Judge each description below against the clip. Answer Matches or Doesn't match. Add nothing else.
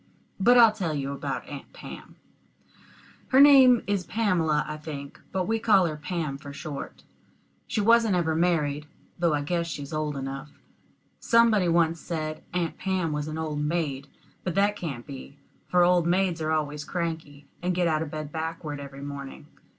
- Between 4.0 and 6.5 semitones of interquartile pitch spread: Doesn't match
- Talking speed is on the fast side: Doesn't match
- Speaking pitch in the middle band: Matches